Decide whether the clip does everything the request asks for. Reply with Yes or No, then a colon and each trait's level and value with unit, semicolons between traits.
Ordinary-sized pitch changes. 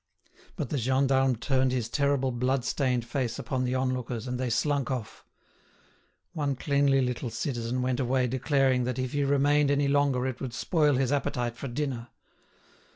No: narrow, 2.0 semitones